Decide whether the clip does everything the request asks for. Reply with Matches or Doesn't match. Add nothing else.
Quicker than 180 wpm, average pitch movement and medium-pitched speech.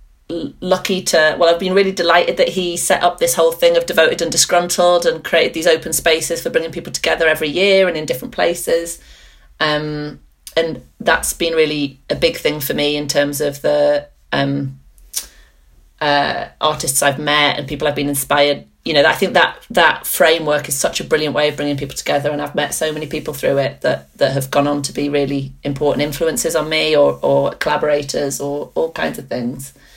Matches